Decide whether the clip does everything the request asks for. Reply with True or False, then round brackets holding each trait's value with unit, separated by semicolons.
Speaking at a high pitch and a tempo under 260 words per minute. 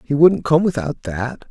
False (145 Hz; 200 wpm)